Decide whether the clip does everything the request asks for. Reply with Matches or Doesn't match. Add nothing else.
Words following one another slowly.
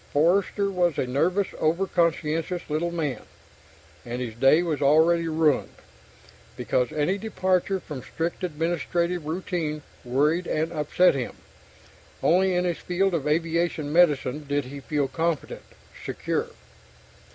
Matches